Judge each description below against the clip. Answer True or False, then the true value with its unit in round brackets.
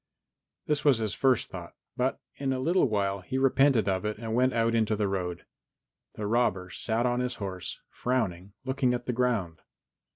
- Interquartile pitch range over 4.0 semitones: True (4.4 semitones)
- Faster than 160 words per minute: True (190 wpm)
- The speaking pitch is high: False (115 Hz)